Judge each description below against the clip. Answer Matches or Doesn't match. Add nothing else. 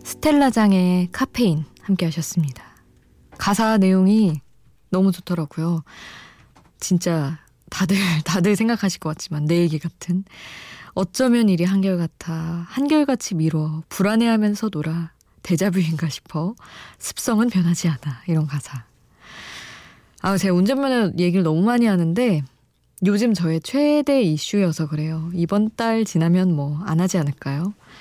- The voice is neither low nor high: Matches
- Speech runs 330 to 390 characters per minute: Doesn't match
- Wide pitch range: Doesn't match